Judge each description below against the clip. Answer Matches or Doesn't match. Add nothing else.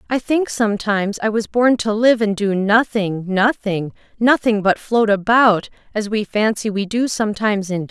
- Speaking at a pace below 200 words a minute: Matches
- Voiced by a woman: Matches